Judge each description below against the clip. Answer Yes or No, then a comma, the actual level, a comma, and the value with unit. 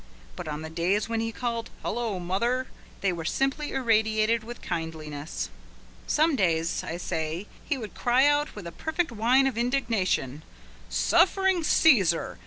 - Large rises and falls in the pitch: Yes, wide, 7.4 semitones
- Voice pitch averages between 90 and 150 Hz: No, high, 225 Hz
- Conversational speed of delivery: Yes, average, 150 wpm